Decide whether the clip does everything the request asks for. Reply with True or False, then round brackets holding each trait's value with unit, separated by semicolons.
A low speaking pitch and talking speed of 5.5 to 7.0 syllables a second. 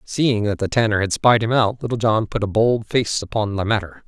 False (110 Hz; 5.3 syllables/s)